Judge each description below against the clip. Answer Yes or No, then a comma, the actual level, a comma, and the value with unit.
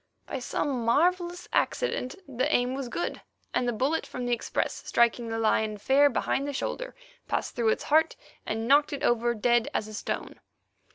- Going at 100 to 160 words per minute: No, average, 180 wpm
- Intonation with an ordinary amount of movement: Yes, average, 3.7 semitones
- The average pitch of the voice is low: No, high, 245 Hz